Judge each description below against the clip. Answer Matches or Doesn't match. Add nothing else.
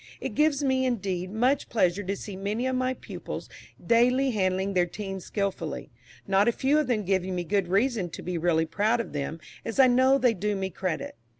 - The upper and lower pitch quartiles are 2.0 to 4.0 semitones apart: Doesn't match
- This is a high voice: Matches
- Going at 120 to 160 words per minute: Doesn't match